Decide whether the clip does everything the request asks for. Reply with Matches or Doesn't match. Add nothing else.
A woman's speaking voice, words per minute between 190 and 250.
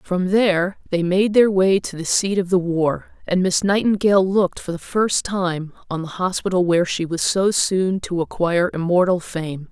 Matches